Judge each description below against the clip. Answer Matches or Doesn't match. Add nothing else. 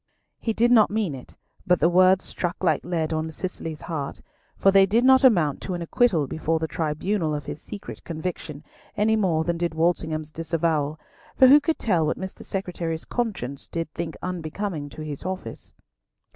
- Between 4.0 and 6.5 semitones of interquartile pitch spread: Doesn't match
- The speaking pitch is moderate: Matches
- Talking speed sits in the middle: Matches